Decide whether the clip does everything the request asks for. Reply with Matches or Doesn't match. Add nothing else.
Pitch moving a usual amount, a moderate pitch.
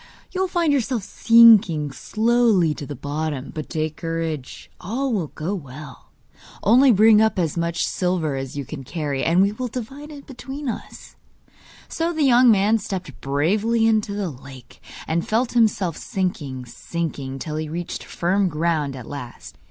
Doesn't match